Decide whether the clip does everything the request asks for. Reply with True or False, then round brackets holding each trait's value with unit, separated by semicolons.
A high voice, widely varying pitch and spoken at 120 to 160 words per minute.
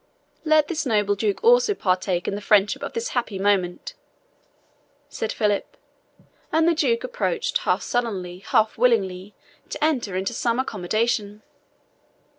True (220 Hz; 7.1 semitones; 135 wpm)